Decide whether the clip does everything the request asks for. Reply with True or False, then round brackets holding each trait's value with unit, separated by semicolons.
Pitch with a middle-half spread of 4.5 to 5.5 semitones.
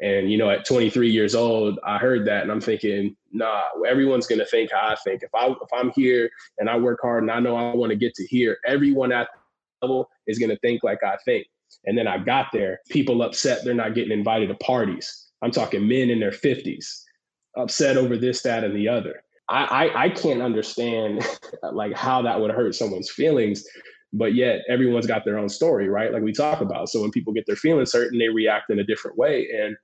False (2.7 semitones)